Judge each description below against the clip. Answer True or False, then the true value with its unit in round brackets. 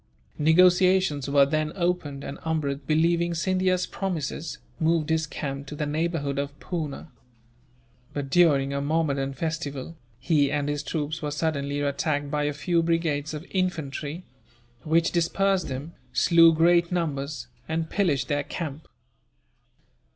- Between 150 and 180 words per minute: False (135 wpm)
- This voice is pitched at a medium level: True (155 Hz)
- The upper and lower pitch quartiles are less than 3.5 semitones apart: True (2.9 semitones)